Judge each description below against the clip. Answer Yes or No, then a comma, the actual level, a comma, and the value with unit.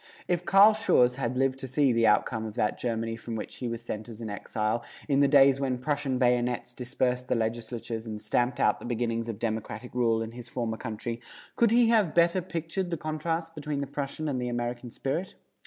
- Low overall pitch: Yes, low, 125 Hz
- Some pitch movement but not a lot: Yes, average, 4.0 semitones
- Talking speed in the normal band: No, fast, 210 wpm